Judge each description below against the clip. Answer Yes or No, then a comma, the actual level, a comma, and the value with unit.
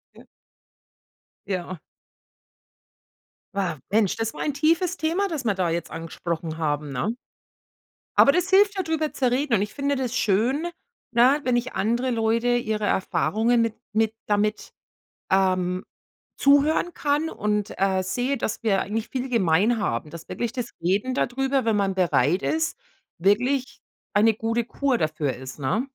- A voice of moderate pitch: No, high, 225 Hz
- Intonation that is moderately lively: No, wide, 5.8 semitones